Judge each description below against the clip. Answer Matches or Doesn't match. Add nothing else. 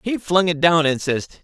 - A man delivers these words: Matches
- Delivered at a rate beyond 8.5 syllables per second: Doesn't match